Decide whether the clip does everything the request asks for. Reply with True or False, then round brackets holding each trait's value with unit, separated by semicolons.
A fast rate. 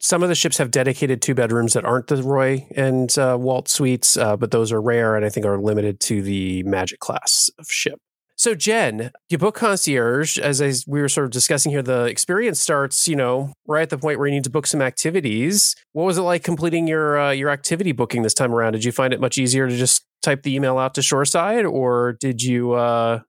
True (240 wpm)